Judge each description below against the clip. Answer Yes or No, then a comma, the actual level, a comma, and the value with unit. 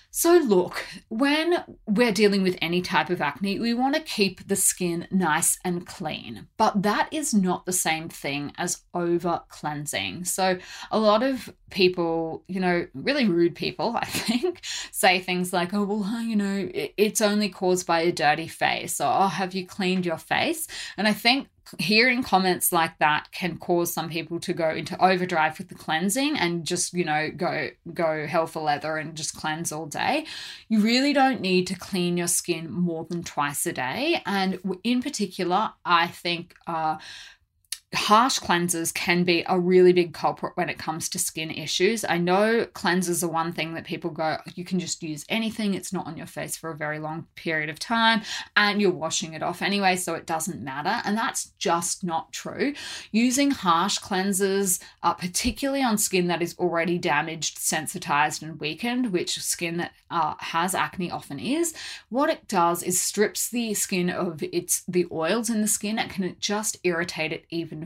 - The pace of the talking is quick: No, average, 185 wpm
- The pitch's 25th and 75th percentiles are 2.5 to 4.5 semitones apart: Yes, average, 3.7 semitones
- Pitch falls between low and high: Yes, medium, 180 Hz